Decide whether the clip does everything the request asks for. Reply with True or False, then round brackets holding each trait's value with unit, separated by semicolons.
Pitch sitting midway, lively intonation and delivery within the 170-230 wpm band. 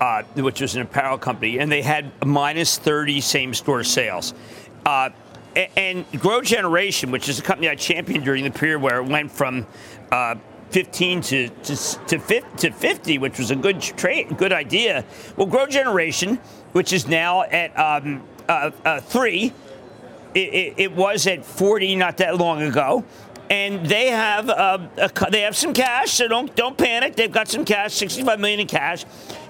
True (175 Hz; 6.3 semitones; 180 wpm)